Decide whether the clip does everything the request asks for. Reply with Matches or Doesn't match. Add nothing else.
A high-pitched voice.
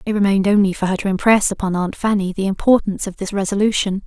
Matches